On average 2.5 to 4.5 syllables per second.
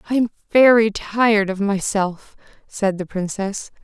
Yes: 4.3 syllables/s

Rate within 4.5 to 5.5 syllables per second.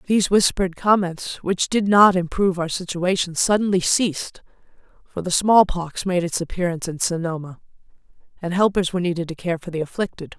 No: 5.7 syllables/s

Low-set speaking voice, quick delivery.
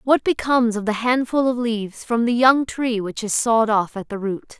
No: high, 230 Hz; fast, 235 wpm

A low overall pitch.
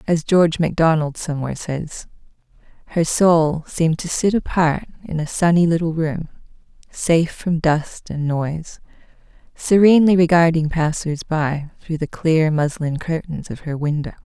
No: medium, 160 Hz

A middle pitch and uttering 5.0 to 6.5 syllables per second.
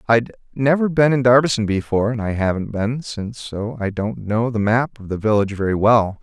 No: low, 115 Hz; 5.5 syllables/s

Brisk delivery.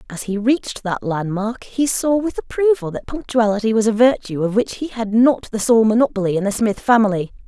Yes: fast, 215 wpm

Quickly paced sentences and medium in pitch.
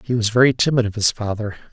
No: fast, 245 wpm; low, 115 Hz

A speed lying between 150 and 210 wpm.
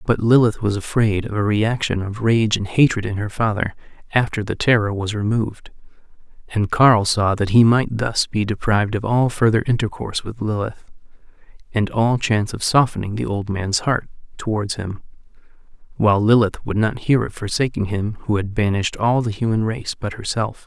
Yes: average, 180 wpm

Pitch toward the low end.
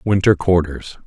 Yes: very low, 90 Hz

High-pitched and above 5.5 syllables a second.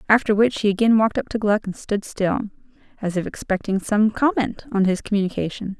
Yes: high, 210 Hz; 5.9 syllables/s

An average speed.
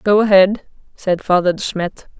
Yes: average, 165 wpm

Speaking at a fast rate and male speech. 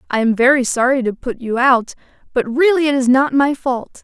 No: fast, 225 wpm; female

